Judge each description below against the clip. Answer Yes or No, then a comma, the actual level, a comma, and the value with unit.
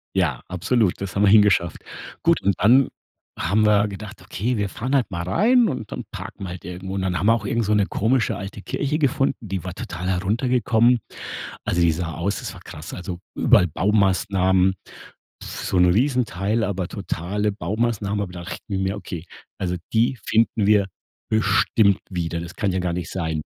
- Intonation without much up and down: No, average, 3.4 semitones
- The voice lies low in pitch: Yes, low, 100 Hz